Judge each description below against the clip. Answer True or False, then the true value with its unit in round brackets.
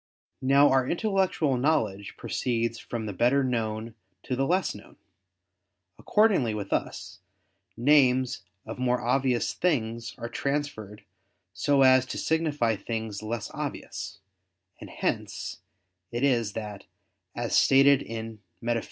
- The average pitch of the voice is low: True (125 Hz)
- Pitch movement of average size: True (3.7 semitones)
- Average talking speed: False (125 wpm)